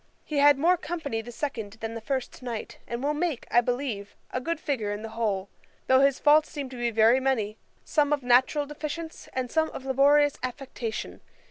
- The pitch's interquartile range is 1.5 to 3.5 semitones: No, average, 4.2 semitones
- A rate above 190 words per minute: Yes, average, 200 wpm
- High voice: Yes, very high, 260 Hz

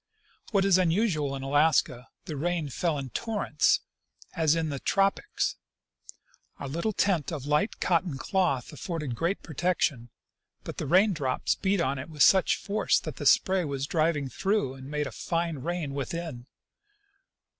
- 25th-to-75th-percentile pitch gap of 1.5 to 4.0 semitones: No, average, 4.7 semitones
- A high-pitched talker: No, medium, 160 Hz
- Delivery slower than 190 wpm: Yes, average, 155 wpm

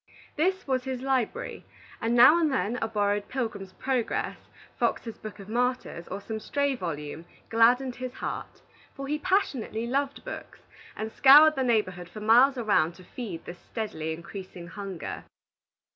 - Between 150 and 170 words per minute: Yes, average, 155 wpm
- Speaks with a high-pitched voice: Yes, high, 230 Hz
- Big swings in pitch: No, average, 4.8 semitones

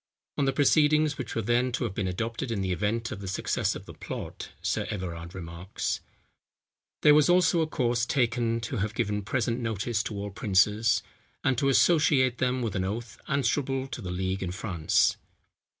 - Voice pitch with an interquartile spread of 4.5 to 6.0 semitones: Yes, average, 4.8 semitones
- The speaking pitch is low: Yes, low, 115 Hz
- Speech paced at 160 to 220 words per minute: Yes, average, 180 wpm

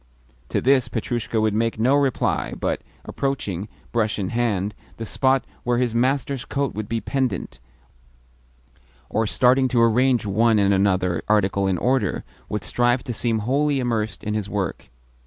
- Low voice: Yes, low, 115 Hz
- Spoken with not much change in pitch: No, average, 3.4 semitones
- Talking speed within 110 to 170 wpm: Yes, average, 155 wpm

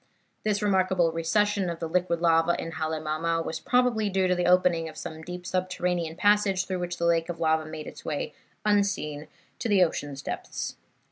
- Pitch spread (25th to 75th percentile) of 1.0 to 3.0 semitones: Yes, average, 2.7 semitones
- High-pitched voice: No, medium, 175 Hz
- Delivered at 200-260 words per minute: No, average, 185 wpm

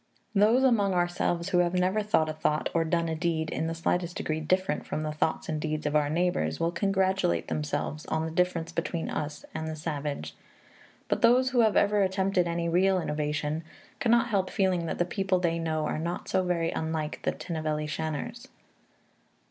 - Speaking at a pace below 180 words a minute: No, average, 190 wpm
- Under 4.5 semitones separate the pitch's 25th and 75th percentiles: Yes, average, 3.2 semitones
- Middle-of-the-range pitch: Yes, medium, 170 Hz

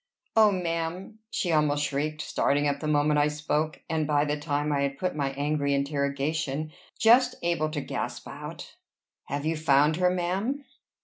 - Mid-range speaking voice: Yes, medium, 150 Hz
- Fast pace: No, average, 170 wpm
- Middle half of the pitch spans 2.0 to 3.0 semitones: Yes, narrow, 2.5 semitones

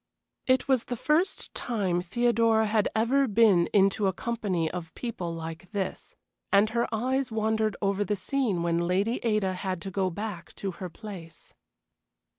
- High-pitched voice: Yes, high, 205 Hz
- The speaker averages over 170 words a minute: No, average, 160 wpm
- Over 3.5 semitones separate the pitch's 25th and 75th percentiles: Yes, average, 4.0 semitones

